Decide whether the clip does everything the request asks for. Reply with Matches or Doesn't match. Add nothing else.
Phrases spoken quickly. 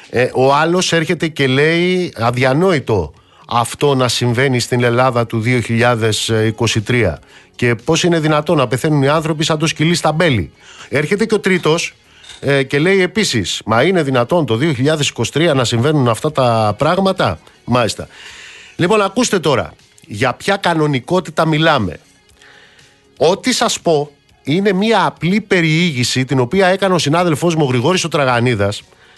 Doesn't match